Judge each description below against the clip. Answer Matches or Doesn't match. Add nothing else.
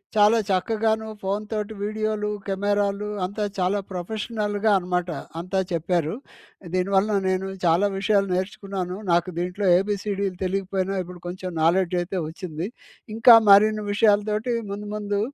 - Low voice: Doesn't match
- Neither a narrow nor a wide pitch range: Doesn't match